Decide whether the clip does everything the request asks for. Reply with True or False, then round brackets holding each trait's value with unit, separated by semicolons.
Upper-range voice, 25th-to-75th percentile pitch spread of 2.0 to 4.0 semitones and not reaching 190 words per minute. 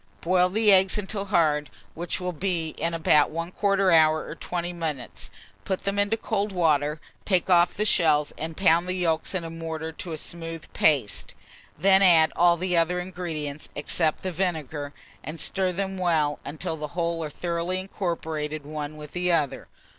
False (170 Hz; 2.9 semitones; 175 wpm)